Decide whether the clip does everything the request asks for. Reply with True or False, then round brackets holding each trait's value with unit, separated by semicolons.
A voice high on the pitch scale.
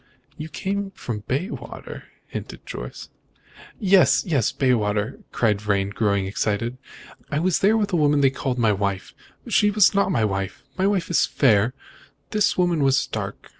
False (135 Hz)